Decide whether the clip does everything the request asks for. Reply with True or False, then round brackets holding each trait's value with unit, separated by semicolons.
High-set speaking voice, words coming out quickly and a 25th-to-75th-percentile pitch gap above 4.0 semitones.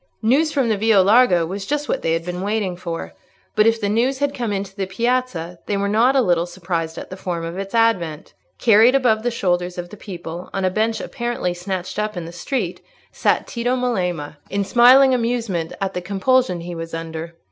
True (195 Hz; 210 wpm; 4.9 semitones)